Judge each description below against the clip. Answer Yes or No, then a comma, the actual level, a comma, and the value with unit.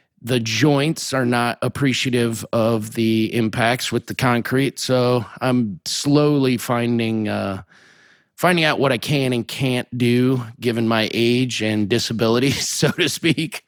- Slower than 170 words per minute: Yes, average, 140 wpm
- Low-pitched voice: Yes, low, 120 Hz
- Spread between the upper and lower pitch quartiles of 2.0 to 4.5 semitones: Yes, narrow, 2.5 semitones